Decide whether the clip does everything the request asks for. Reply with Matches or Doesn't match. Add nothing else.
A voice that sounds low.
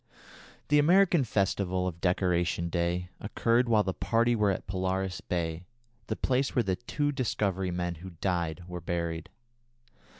Matches